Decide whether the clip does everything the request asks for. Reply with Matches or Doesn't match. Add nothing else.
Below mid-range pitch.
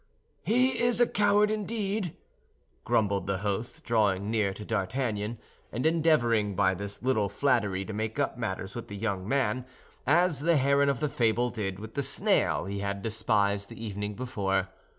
Matches